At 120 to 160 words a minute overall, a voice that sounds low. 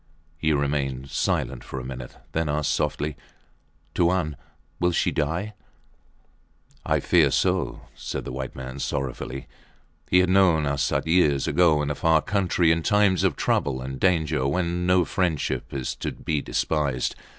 Yes: average, 150 wpm; very low, 75 Hz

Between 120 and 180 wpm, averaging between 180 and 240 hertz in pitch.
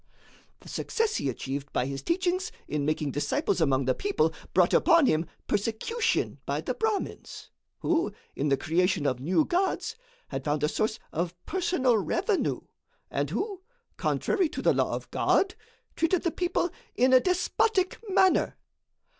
No: average, 155 wpm; very high, 265 Hz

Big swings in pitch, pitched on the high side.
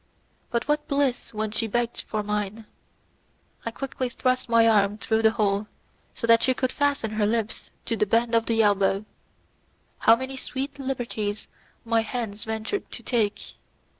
No: average, 2.8 semitones; high, 225 Hz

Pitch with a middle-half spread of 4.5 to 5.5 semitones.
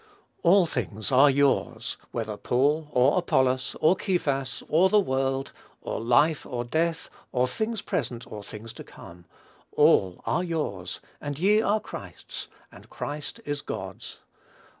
Yes: average, 5.1 semitones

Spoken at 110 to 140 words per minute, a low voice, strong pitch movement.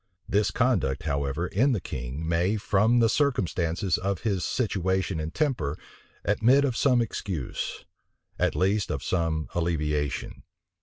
Yes: slow, 135 wpm; very low, 95 Hz; wide, 5.9 semitones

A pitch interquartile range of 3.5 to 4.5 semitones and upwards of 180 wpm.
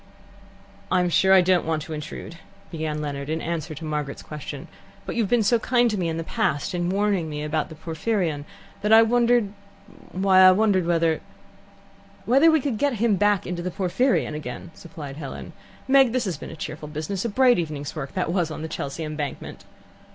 No: average, 5.1 semitones; average, 200 wpm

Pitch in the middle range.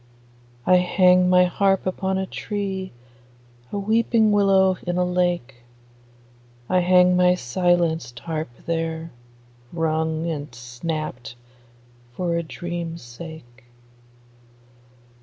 Yes: medium, 175 Hz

